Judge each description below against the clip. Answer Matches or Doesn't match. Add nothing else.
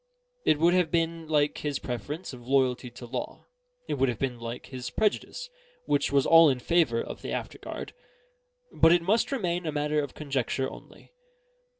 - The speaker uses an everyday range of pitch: Matches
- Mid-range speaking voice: Matches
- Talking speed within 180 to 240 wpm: Matches